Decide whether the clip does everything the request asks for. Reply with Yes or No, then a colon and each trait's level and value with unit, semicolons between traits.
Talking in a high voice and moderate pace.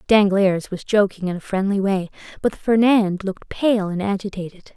Yes: high, 200 Hz; average, 165 wpm